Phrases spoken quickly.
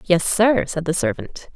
No: average, 195 wpm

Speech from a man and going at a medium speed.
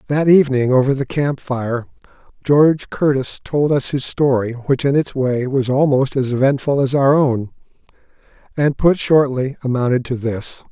Yes: male; average, 160 wpm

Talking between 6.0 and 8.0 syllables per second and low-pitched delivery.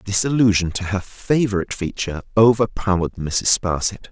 No: 5.4 syllables/s; low, 100 Hz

